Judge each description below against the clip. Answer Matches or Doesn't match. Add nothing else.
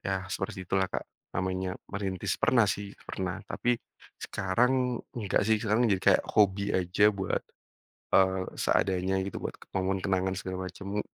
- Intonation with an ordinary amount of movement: Doesn't match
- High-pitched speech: Doesn't match